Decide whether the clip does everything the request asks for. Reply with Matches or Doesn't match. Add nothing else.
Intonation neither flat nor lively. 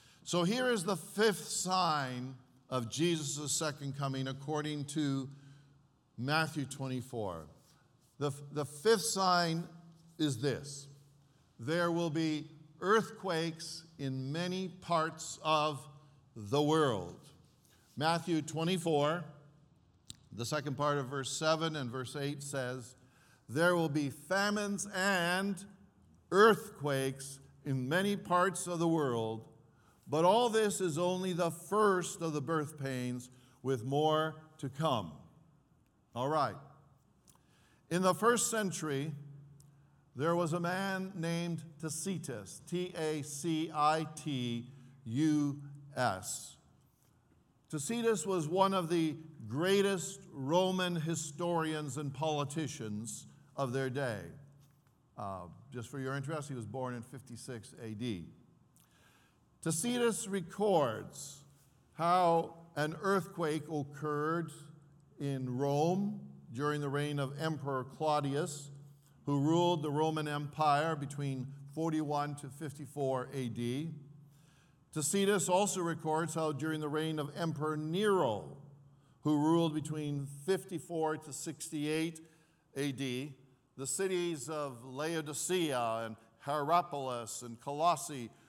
Matches